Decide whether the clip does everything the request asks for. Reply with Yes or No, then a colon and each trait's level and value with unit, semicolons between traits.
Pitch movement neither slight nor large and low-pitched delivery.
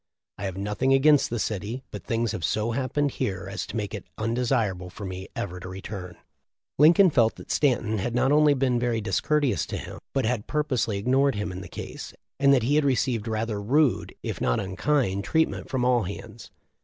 Yes: average, 4.9 semitones; low, 115 Hz